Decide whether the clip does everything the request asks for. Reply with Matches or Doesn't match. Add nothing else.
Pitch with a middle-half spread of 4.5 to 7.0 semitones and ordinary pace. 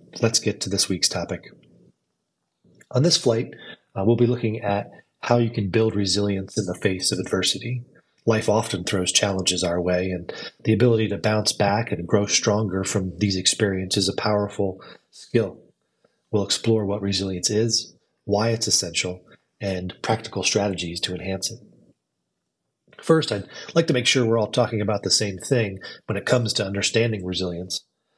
Doesn't match